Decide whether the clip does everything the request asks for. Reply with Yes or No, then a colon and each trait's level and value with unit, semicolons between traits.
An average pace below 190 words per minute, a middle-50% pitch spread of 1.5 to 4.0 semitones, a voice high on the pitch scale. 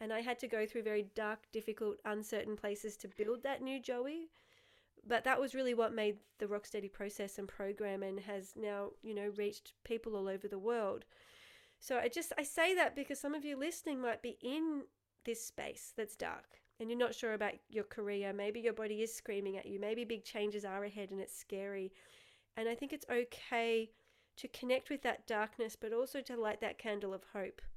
No: fast, 205 wpm; average, 3.2 semitones; high, 220 Hz